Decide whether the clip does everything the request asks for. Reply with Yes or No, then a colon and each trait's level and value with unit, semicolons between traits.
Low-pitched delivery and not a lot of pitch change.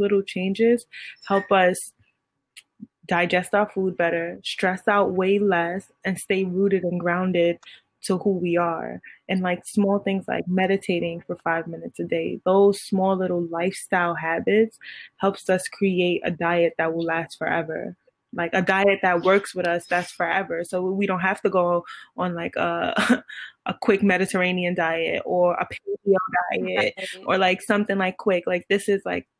No: medium, 185 Hz; narrow, 2.1 semitones